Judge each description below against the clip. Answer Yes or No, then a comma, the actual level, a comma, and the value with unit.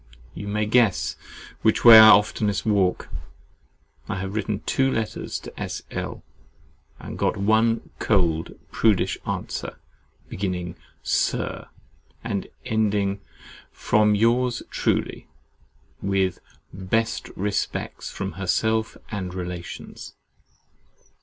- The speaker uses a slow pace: Yes, slow, 100 wpm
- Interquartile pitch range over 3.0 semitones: No, narrow, 2.5 semitones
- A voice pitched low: Yes, low, 105 Hz